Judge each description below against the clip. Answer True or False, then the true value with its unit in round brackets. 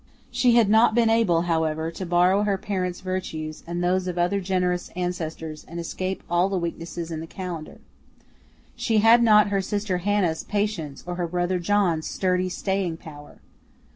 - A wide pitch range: False (2.9 semitones)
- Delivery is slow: False (170 wpm)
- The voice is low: False (180 Hz)